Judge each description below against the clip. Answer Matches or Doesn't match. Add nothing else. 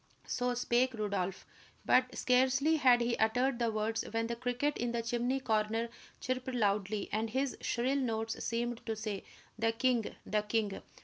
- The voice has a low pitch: Doesn't match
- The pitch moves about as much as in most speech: Doesn't match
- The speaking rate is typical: Matches